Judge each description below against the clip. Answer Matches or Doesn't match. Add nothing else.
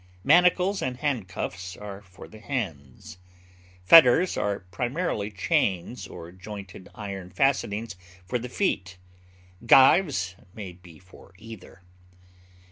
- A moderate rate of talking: Doesn't match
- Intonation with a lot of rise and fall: Matches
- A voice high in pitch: Doesn't match